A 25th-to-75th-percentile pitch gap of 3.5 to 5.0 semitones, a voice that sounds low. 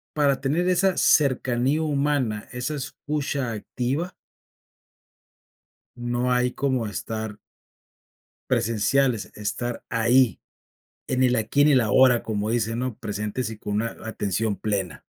Yes: average, 3.9 semitones; low, 125 Hz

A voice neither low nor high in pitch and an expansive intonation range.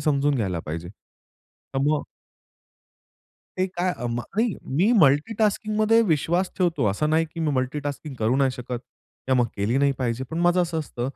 Yes: medium, 145 Hz; wide, 5.7 semitones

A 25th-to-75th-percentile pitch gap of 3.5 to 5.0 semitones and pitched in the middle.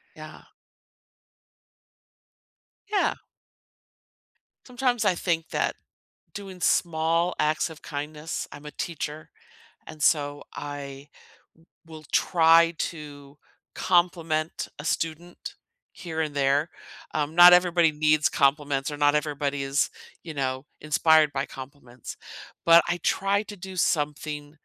No: average, 2.7 semitones; medium, 155 Hz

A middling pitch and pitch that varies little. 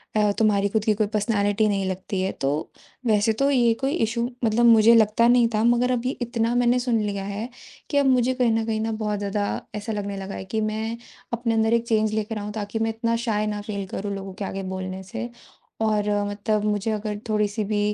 No: high, 215 Hz; narrow, 2.1 semitones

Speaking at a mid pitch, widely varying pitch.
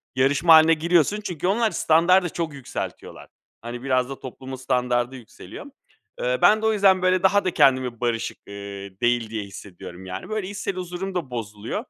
Yes: medium, 145 Hz; wide, 7.2 semitones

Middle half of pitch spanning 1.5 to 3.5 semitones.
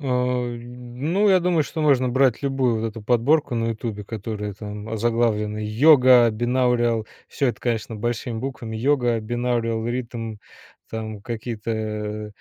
Yes: narrow, 2.4 semitones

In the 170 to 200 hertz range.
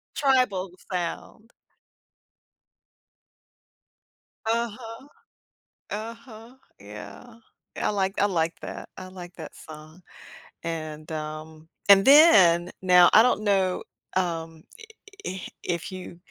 Yes: medium, 185 Hz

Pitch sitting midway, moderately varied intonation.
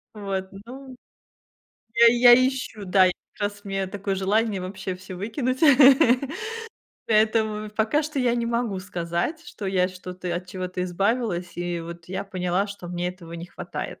No: high, 195 Hz; average, 3.8 semitones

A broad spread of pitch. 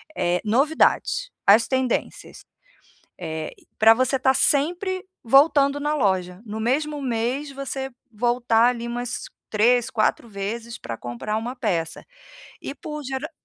No: average, 4.3 semitones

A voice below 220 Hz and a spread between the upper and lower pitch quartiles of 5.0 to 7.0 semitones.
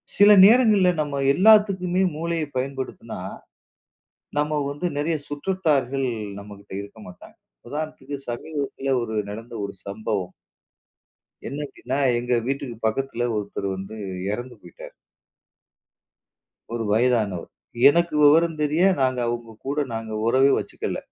Yes: low, 135 Hz; wide, 5.4 semitones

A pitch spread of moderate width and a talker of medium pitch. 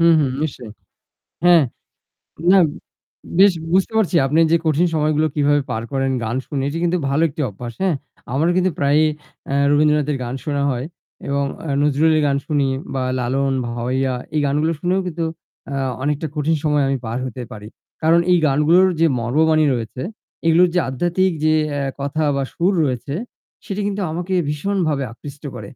Yes: average, 3.6 semitones; medium, 150 Hz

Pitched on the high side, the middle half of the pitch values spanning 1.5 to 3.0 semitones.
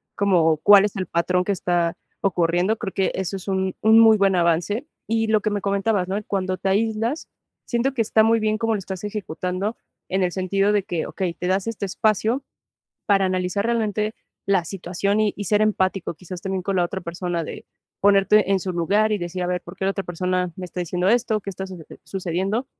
Yes: high, 195 Hz; average, 2.7 semitones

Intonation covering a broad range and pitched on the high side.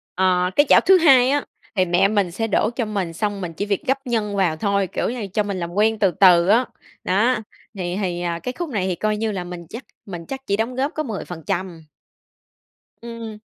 No: average, 4.4 semitones; high, 205 Hz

